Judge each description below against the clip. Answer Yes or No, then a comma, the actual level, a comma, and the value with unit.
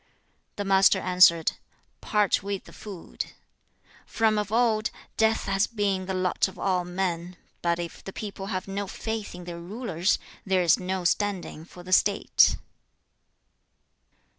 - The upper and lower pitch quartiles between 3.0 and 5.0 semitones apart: No, narrow, 2.4 semitones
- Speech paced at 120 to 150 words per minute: Yes, average, 145 wpm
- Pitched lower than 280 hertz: Yes, high, 190 Hz